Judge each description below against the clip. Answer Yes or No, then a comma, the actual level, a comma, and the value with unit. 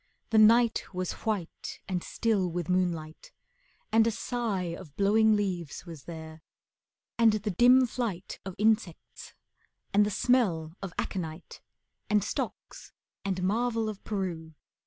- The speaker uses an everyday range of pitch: Yes, average, 4.1 semitones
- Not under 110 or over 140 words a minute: Yes, slow, 135 wpm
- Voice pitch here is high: Yes, high, 195 Hz